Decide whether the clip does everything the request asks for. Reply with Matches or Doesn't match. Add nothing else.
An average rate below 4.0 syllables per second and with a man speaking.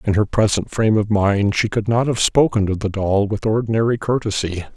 Doesn't match